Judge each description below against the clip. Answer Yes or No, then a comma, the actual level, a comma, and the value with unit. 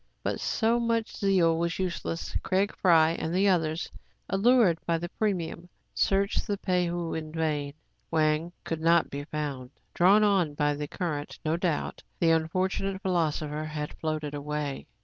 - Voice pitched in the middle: Yes, medium, 165 Hz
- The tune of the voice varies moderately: Yes, average, 3.5 semitones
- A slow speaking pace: No, average, 160 wpm